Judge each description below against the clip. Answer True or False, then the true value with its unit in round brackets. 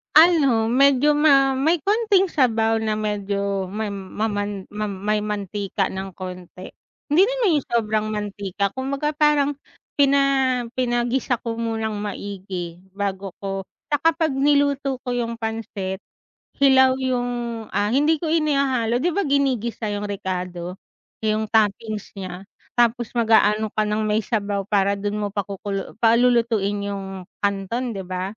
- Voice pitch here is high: True (220 Hz)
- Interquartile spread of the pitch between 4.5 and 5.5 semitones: True (4.8 semitones)